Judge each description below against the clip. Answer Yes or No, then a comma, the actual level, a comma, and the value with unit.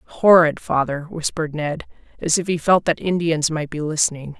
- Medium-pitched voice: Yes, medium, 160 Hz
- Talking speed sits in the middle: Yes, average, 180 wpm